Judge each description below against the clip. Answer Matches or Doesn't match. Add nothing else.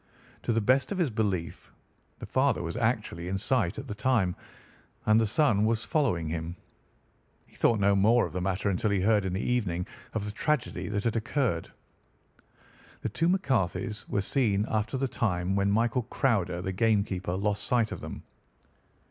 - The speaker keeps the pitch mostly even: Doesn't match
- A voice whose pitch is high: Doesn't match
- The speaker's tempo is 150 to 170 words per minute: Doesn't match